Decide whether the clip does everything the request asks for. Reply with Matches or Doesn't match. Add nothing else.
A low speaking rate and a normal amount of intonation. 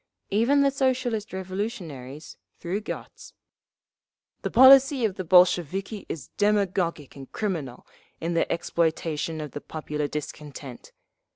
Doesn't match